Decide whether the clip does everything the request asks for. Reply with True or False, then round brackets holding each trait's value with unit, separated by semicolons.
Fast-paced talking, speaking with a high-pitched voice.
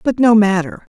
False (190 wpm; 210 Hz)